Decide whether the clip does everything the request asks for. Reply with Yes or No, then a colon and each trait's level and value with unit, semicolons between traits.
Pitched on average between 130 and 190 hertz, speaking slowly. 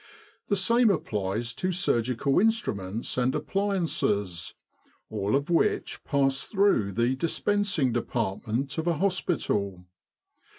Yes: low, 135 Hz; slow, 110 wpm